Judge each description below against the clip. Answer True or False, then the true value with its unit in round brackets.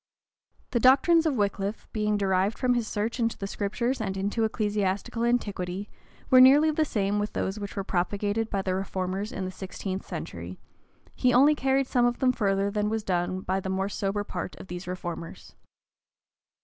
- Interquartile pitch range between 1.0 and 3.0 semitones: False (3.8 semitones)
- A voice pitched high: True (205 Hz)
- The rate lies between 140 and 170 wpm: False (180 wpm)